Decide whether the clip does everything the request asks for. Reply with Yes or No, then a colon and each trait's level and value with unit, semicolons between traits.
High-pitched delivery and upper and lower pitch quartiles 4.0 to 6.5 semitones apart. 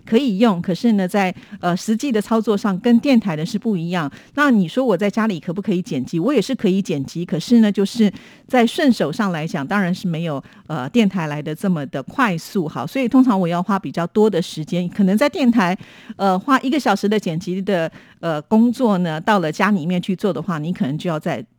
Yes: high, 195 Hz; average, 4.3 semitones